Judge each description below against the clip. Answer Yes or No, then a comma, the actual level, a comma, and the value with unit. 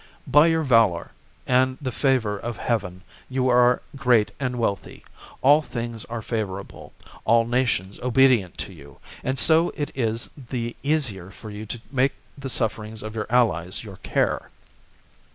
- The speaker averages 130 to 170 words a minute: Yes, average, 150 wpm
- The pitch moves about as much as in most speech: Yes, average, 3.6 semitones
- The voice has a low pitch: Yes, low, 120 Hz